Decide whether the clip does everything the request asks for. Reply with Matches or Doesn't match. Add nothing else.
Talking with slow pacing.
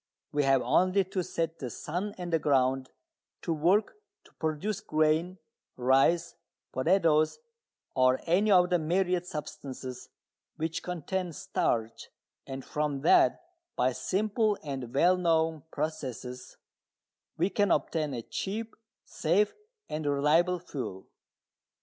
Matches